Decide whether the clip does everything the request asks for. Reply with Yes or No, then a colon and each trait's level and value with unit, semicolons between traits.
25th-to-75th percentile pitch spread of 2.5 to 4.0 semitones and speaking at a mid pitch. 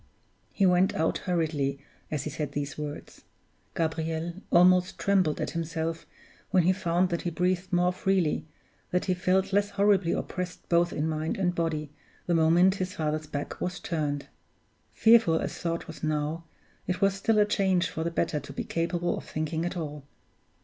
Yes: average, 2.8 semitones; medium, 170 Hz